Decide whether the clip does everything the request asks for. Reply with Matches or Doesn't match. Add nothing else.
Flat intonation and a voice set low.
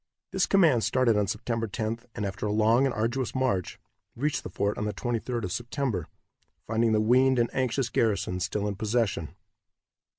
Doesn't match